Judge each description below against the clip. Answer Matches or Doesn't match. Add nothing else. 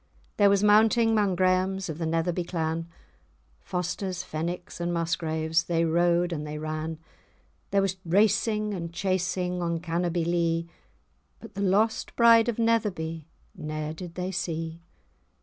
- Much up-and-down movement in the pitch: Doesn't match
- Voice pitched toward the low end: Doesn't match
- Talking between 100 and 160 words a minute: Matches